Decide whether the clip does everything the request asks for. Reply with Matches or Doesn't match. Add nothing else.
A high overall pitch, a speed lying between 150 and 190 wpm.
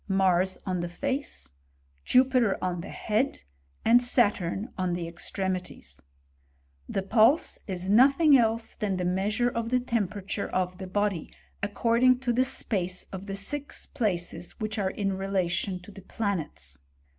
Matches